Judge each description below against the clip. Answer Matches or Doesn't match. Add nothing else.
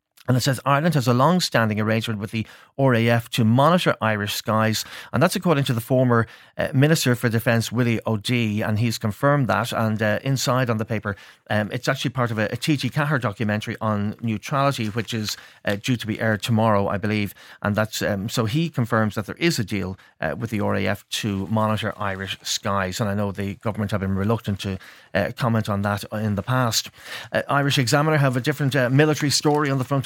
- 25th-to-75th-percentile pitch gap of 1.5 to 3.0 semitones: Doesn't match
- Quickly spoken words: Matches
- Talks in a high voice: Doesn't match